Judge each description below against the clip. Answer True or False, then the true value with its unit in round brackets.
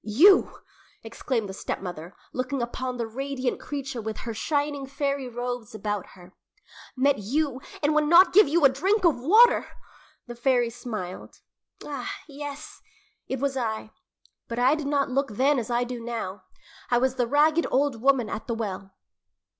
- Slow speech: False (165 wpm)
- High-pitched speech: True (255 Hz)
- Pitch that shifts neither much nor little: True (3.8 semitones)